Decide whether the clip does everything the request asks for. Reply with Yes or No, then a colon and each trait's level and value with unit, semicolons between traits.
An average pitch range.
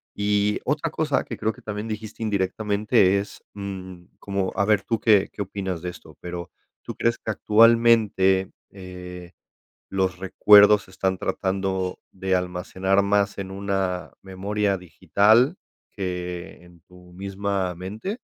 No: narrow, 2.1 semitones